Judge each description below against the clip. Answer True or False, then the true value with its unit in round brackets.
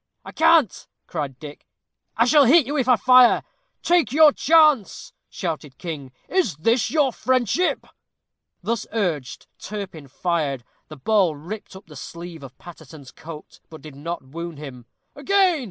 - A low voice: False (180 Hz)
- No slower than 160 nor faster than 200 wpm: False (150 wpm)